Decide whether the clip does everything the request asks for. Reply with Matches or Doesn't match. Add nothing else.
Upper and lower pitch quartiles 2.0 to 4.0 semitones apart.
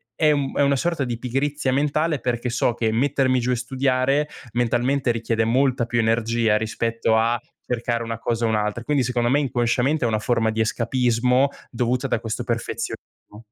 Matches